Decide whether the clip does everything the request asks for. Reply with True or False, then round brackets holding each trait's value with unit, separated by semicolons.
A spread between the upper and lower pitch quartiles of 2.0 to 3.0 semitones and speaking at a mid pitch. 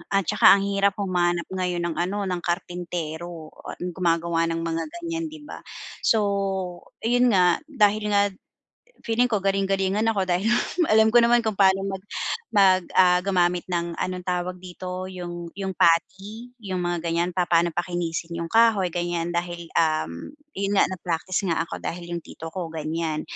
True (2.4 semitones; 180 Hz)